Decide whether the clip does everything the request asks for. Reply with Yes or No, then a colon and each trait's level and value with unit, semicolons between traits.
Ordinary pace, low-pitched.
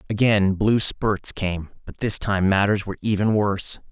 Yes: average, 170 wpm; low, 100 Hz